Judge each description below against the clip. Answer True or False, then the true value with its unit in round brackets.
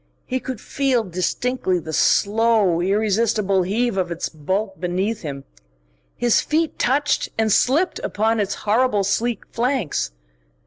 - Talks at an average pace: False (130 wpm)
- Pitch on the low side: False (215 Hz)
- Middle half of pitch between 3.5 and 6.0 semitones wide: True (4.5 semitones)